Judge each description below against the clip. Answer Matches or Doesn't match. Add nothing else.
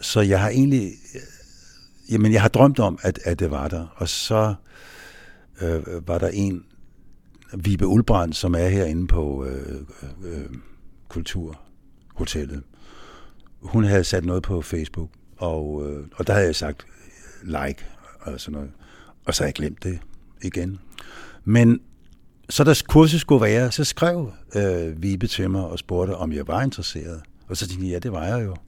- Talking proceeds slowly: Doesn't match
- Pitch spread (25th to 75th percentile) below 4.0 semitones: Doesn't match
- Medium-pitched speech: Doesn't match